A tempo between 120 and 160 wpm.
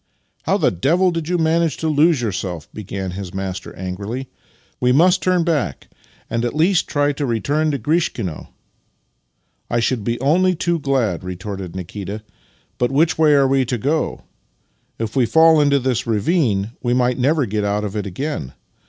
No: average, 190 wpm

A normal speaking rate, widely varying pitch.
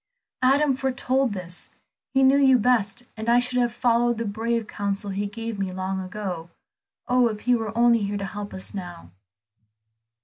No: average, 175 wpm; average, 3.7 semitones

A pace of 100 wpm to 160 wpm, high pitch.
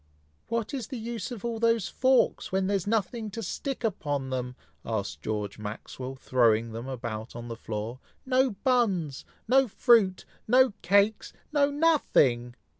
Yes: average, 155 wpm; high, 195 Hz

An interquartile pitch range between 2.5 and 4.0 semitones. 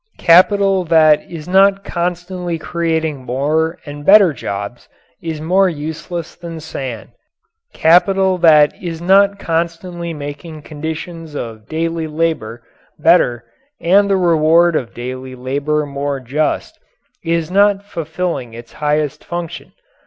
Yes: average, 3.2 semitones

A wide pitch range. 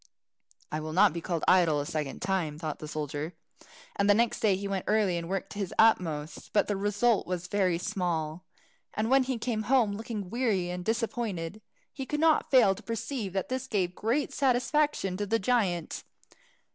No: average, 4.7 semitones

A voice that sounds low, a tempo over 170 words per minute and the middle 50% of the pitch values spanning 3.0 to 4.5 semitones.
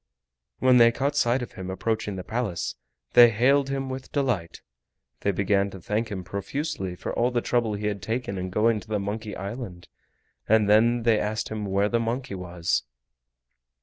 Yes: low, 110 Hz; average, 180 wpm; average, 3.6 semitones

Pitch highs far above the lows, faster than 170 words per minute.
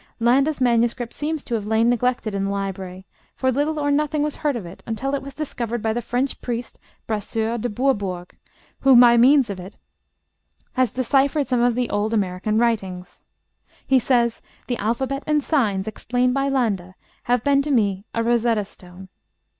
No: average, 4.3 semitones; average, 180 wpm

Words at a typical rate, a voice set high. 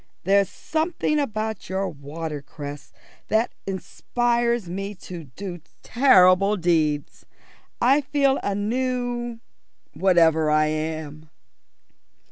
No: slow, 95 wpm; high, 195 Hz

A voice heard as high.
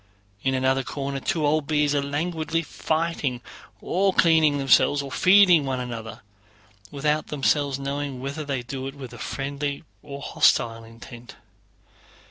No: medium, 140 Hz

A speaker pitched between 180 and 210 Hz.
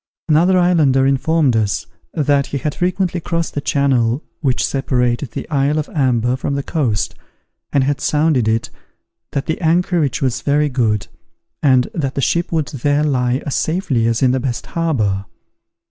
No: medium, 140 Hz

